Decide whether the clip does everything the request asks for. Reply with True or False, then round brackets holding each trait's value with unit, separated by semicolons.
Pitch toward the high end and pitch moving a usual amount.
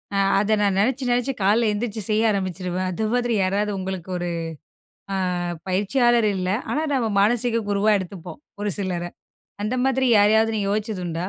True (210 Hz; 3.6 semitones)